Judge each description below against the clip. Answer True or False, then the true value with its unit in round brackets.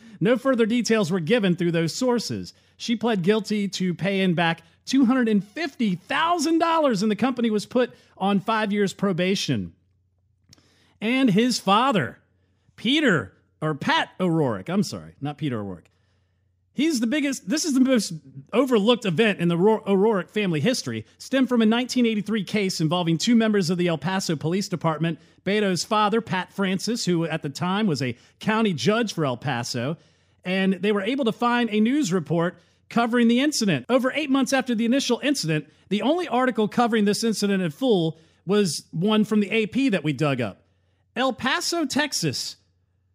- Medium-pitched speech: False (200 Hz)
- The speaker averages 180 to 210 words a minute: False (165 wpm)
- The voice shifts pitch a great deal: True (6.7 semitones)